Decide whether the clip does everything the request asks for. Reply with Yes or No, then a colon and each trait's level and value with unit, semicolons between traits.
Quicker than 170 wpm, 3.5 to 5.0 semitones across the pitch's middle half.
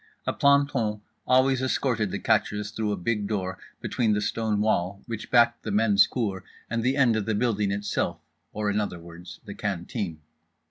No: average, 180 wpm; average, 2.8 semitones